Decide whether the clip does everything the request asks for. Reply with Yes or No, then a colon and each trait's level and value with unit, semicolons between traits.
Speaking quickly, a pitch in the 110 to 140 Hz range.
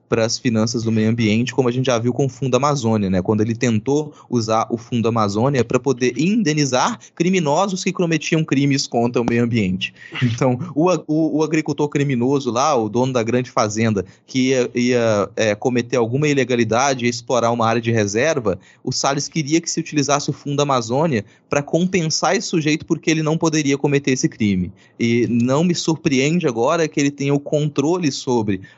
Yes: fast, 190 wpm; low, 135 Hz